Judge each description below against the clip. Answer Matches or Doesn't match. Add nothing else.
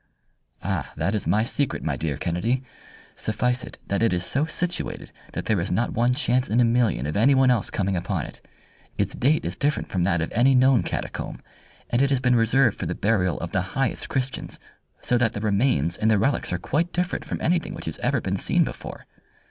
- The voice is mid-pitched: Doesn't match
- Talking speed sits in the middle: Doesn't match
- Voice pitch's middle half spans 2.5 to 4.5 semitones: Doesn't match